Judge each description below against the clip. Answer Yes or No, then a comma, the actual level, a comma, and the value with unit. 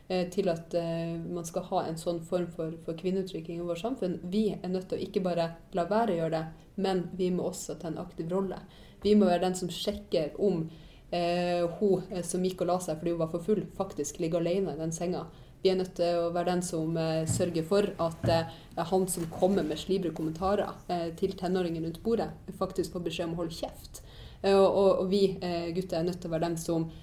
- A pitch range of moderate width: No, narrow, 2.1 semitones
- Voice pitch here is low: No, medium, 175 Hz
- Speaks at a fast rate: Yes, fast, 230 wpm